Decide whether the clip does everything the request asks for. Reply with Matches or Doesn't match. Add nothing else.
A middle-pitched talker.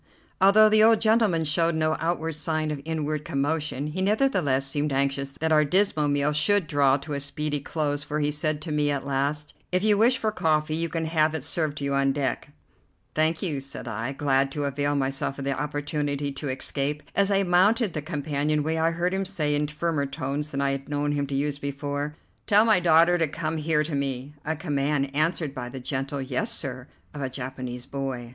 Matches